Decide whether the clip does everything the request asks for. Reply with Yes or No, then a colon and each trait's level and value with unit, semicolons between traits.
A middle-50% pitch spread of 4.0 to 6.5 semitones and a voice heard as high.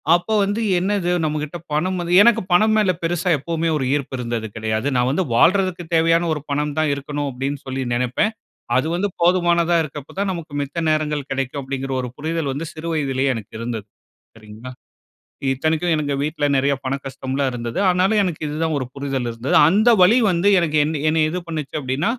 No: average, 4.4 semitones; medium, 150 Hz